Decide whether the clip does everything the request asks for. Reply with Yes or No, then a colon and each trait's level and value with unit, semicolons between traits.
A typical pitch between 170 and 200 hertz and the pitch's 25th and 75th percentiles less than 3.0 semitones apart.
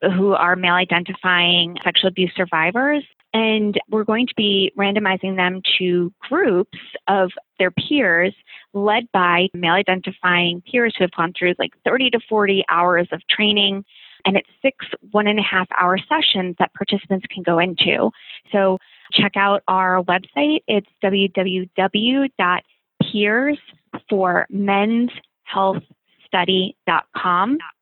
Yes: high, 190 Hz; narrow, 2.6 semitones